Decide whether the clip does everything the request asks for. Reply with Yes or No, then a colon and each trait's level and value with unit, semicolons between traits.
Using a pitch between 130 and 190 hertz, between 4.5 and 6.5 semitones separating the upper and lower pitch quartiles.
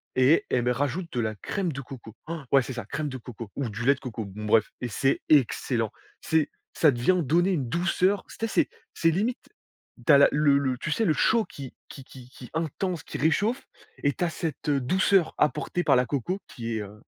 Yes: medium, 140 Hz; average, 5.2 semitones